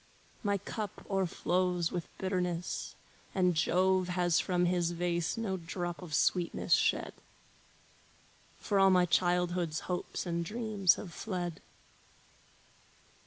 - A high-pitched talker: No, medium, 180 Hz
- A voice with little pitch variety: Yes, narrow, 1.4 semitones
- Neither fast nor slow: No, slow, 115 wpm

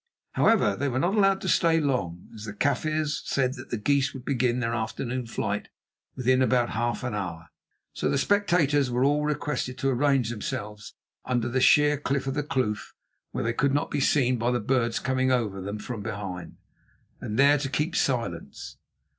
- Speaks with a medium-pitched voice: No, low, 130 Hz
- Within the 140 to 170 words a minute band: No, average, 190 wpm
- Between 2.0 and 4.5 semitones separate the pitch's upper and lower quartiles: Yes, average, 3.7 semitones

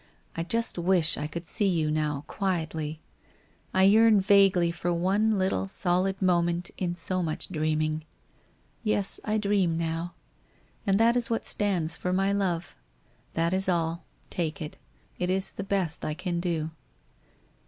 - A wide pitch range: No, average, 3.0 semitones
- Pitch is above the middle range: No, medium, 175 Hz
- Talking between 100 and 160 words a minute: Yes, average, 155 wpm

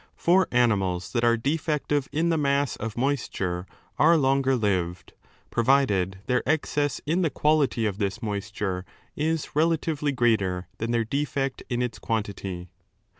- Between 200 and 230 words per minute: No, average, 145 wpm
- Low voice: Yes, low, 125 Hz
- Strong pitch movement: Yes, wide, 6.2 semitones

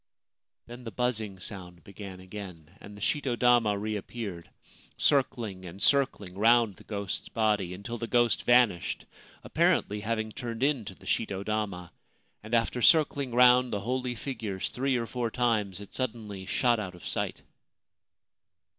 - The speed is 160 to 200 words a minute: No, average, 145 wpm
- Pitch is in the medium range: No, low, 110 Hz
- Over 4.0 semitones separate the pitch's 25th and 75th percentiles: No, average, 3.6 semitones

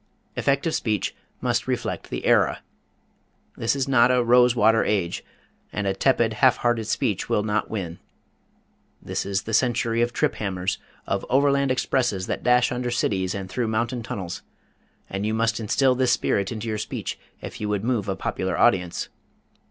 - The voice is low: Yes, low, 115 Hz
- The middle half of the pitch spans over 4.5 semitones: No, average, 3.7 semitones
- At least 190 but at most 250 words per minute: No, average, 170 wpm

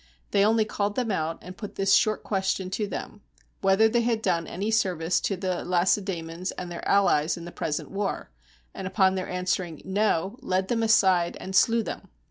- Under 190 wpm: No, average, 200 wpm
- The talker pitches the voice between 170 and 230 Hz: Yes, high, 190 Hz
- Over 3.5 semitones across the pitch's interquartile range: No, narrow, 2.6 semitones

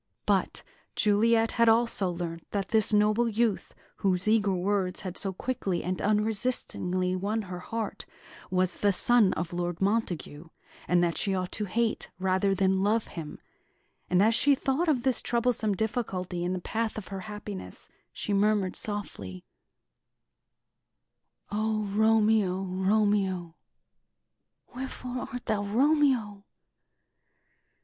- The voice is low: No, high, 205 Hz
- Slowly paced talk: Yes, slow, 130 wpm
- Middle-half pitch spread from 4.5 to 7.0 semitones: No, average, 3.2 semitones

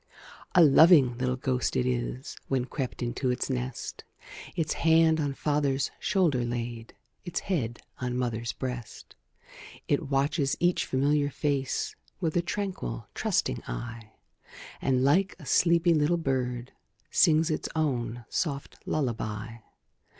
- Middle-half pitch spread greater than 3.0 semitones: Yes, average, 4.6 semitones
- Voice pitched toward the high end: No, low, 135 Hz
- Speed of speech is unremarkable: No, slow, 130 wpm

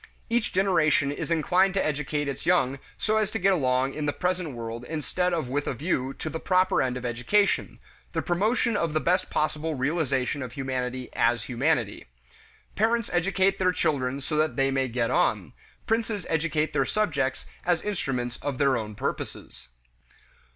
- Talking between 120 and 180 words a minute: Yes, average, 170 wpm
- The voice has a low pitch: No, medium, 150 Hz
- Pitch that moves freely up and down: Yes, wide, 5.9 semitones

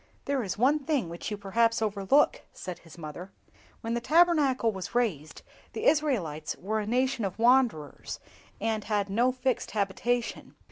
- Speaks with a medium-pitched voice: No, high, 225 Hz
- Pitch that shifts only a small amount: No, average, 5.0 semitones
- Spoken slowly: No, average, 155 wpm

